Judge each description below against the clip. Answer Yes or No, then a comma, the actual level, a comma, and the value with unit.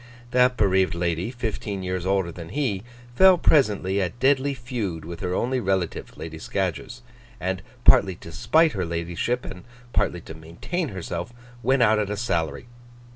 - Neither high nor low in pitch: No, very low, 95 Hz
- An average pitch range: No, wide, 5.9 semitones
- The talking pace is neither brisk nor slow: Yes, average, 160 wpm